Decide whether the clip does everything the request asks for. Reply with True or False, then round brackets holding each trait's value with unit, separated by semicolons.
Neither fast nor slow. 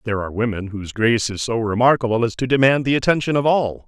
False (230 wpm)